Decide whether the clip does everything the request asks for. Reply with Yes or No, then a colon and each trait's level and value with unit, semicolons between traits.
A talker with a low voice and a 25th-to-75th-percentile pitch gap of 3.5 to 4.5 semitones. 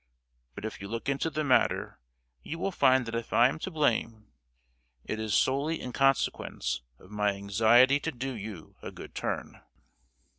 Yes: low, 120 Hz; average, 4.2 semitones